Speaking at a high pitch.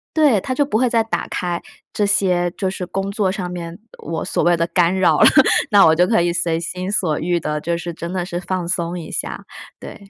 No: medium, 180 Hz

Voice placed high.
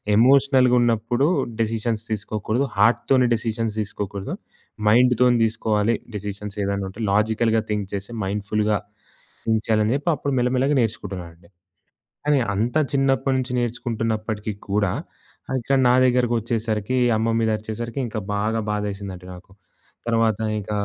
No: low, 110 Hz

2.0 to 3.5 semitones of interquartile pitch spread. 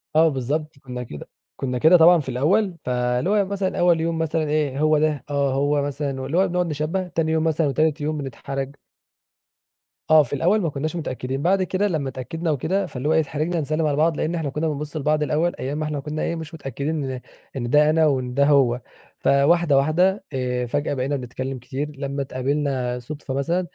Yes: average, 3.1 semitones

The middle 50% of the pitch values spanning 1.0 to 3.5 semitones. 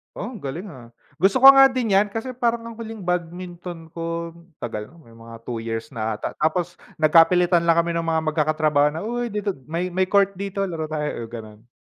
No: average, 4.8 semitones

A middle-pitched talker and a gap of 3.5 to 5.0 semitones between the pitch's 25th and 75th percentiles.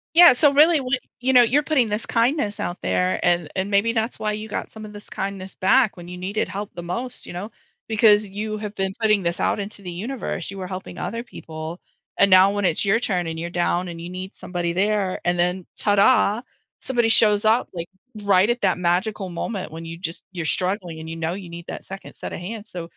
No: high, 195 Hz; average, 3.8 semitones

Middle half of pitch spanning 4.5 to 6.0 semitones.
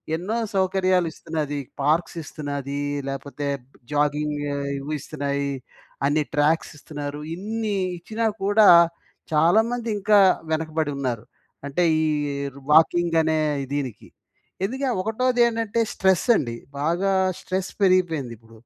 Yes: average, 5.2 semitones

